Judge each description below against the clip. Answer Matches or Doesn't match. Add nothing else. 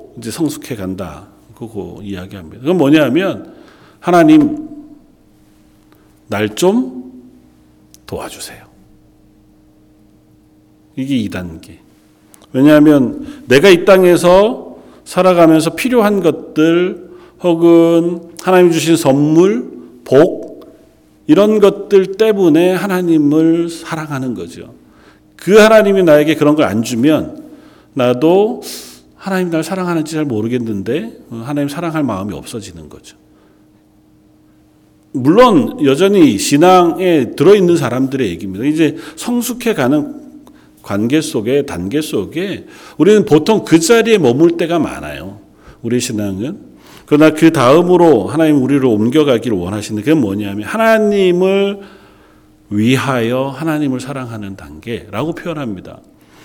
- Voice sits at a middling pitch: Matches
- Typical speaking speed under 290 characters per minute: Matches